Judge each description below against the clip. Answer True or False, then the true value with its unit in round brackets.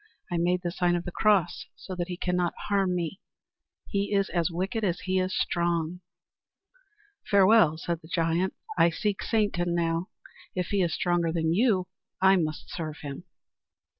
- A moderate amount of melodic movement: False (2.1 semitones)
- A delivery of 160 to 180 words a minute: True (165 wpm)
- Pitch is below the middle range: False (175 Hz)